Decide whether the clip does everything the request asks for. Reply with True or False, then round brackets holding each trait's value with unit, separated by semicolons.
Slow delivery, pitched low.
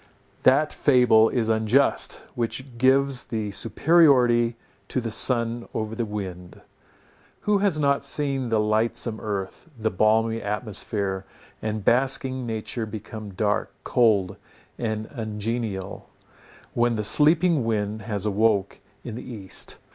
True (125 wpm; 115 Hz)